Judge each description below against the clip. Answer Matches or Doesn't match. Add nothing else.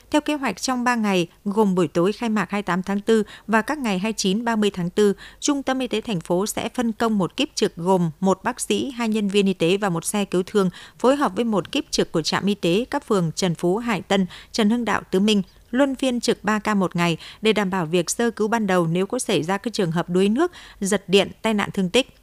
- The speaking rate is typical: Doesn't match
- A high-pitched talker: Matches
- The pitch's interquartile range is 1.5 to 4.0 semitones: Matches